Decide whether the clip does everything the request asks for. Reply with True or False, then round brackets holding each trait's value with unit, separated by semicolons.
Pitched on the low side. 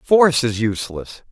True (130 Hz)